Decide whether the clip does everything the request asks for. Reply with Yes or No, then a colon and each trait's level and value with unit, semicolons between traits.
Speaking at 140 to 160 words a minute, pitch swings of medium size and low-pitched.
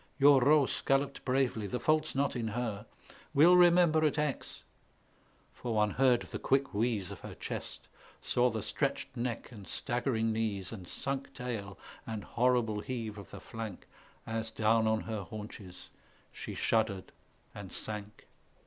Yes: average, 150 wpm; average, 4.1 semitones; low, 115 Hz